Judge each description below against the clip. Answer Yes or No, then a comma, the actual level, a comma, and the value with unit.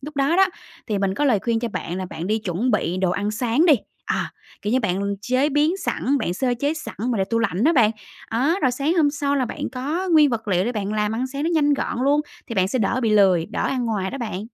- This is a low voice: No, high, 240 Hz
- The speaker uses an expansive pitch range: Yes, wide, 5.7 semitones